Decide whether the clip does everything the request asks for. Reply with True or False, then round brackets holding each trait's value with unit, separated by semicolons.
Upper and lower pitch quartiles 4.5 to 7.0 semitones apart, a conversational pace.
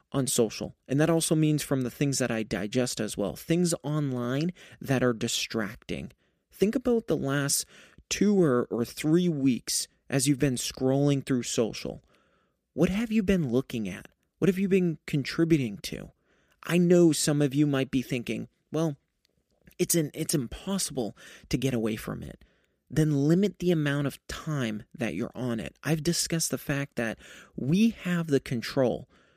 True (4.8 semitones; 170 wpm)